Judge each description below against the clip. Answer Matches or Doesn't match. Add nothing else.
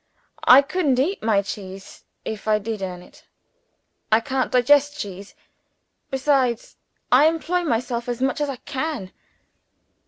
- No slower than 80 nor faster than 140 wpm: Matches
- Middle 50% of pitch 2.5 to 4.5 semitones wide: Doesn't match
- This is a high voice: Matches